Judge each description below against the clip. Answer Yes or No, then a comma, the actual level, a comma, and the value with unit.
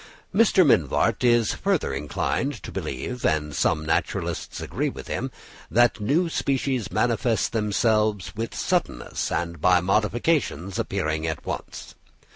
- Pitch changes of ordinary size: No, wide, 6.7 semitones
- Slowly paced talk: Yes, slow, 125 wpm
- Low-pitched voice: Yes, low, 110 Hz